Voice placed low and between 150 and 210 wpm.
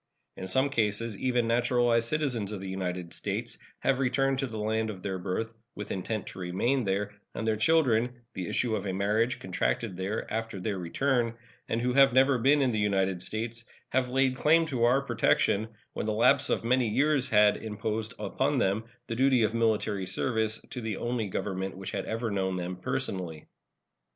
Yes: low, 110 Hz; average, 190 wpm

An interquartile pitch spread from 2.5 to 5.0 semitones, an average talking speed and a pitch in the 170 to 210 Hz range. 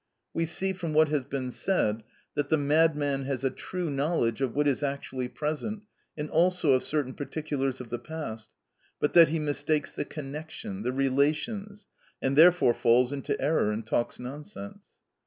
No: average, 3.5 semitones; average, 170 wpm; medium, 145 Hz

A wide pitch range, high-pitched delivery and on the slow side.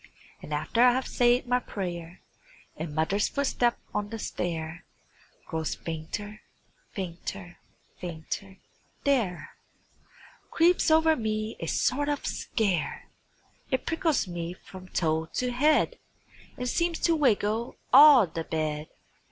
Yes: wide, 7.1 semitones; high, 205 Hz; slow, 120 wpm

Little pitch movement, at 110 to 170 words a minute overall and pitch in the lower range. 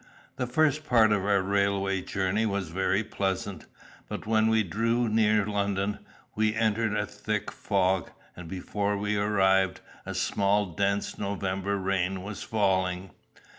Yes: narrow, 1.9 semitones; average, 140 wpm; low, 100 Hz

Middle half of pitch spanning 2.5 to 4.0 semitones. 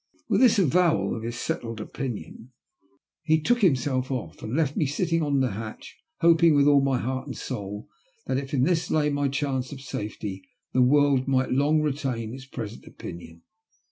Yes: average, 3.6 semitones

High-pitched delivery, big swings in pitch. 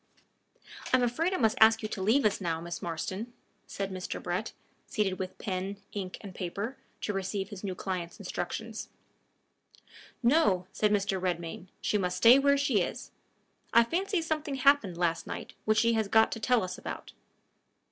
No: high, 205 Hz; average, 4.3 semitones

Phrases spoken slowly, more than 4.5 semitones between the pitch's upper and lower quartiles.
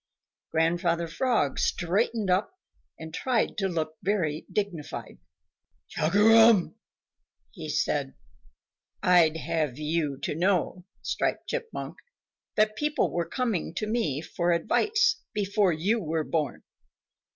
Yes: slow, 110 wpm; average, 5.0 semitones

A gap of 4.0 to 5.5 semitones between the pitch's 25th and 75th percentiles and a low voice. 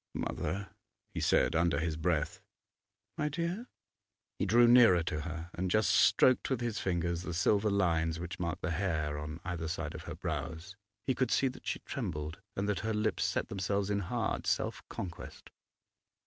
Yes: average, 4.5 semitones; very low, 90 Hz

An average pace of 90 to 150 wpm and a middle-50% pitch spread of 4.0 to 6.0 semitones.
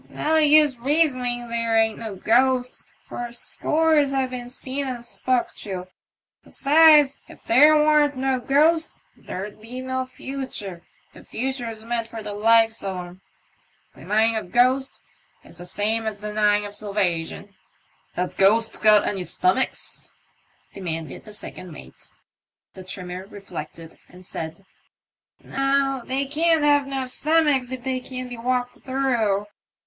Yes: average, 145 wpm; average, 4.6 semitones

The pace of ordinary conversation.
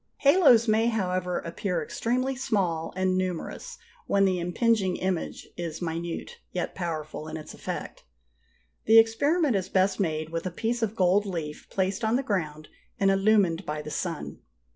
Yes: average, 160 wpm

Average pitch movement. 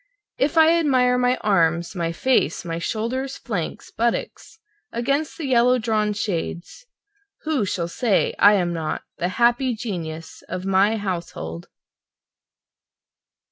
No: wide, 6.4 semitones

